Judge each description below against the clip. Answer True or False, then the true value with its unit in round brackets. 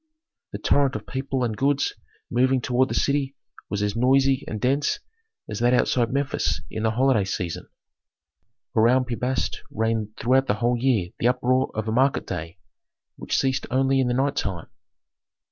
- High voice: False (125 Hz)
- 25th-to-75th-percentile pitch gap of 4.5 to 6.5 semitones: False (3.2 semitones)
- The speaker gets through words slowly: False (170 wpm)